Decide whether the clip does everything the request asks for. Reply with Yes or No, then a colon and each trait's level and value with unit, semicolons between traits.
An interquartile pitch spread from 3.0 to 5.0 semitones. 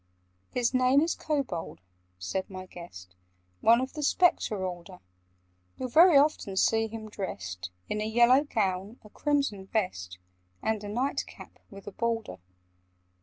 No: wide, 5.5 semitones